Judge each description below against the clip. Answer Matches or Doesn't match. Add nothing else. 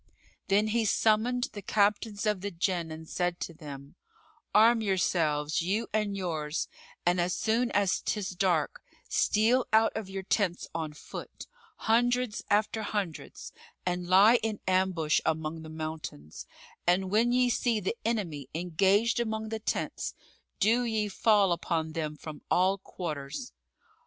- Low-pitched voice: Doesn't match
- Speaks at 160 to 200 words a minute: Doesn't match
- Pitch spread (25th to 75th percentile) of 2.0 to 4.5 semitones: Doesn't match